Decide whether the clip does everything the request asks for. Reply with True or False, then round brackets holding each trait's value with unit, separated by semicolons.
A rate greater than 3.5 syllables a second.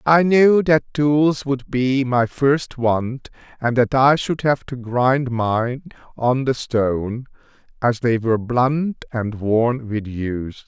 False (3.4 syllables/s)